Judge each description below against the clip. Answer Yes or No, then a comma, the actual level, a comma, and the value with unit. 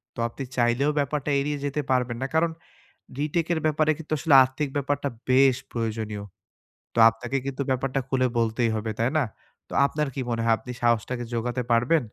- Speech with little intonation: No, average, 3.5 semitones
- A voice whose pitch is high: No, low, 130 Hz